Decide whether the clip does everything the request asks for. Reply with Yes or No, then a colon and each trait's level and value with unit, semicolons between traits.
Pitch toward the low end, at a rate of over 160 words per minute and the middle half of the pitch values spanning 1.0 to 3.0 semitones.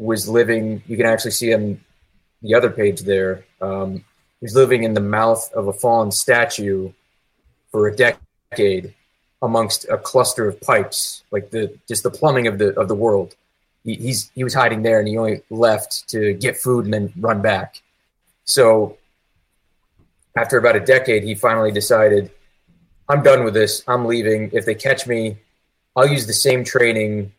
Yes: low, 110 Hz; average, 175 wpm; narrow, 2.5 semitones